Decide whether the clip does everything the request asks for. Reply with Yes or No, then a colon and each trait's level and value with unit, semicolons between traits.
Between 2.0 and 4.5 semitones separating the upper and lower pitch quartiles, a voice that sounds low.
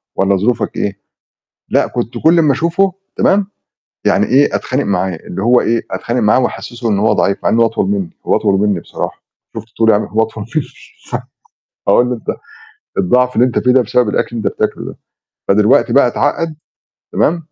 Yes: average, 3.8 semitones; low, 115 Hz